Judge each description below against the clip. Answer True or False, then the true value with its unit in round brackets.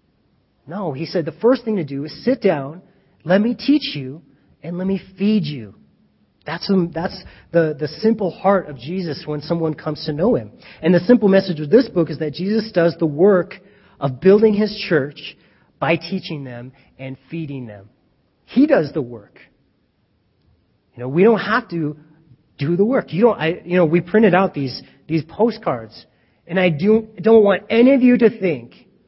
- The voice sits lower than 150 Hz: False (170 Hz)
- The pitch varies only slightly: False (5.3 semitones)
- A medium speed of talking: True (190 wpm)